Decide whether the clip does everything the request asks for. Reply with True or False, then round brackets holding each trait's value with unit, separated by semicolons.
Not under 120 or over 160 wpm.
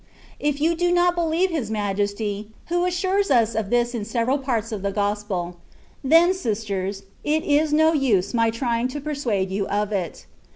False (180 wpm)